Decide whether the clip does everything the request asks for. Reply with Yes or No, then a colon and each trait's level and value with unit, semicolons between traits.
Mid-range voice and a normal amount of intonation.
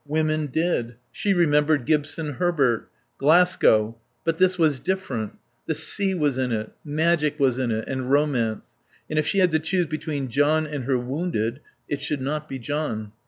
Yes: medium, 150 Hz; average, 3.7 semitones